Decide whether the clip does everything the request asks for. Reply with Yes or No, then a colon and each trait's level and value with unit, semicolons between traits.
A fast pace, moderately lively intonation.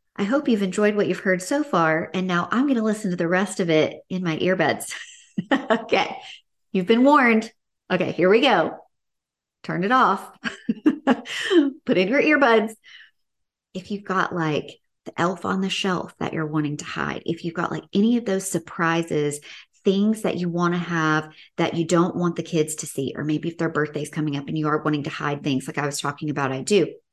No: fast, 210 wpm; wide, 5.8 semitones